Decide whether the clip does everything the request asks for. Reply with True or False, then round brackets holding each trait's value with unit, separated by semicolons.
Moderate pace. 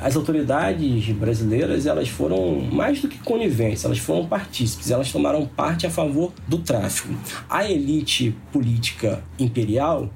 True (135 wpm)